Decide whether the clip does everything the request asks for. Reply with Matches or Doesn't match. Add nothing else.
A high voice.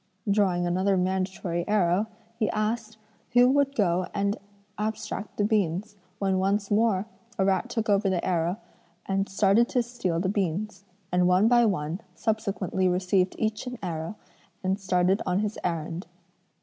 Matches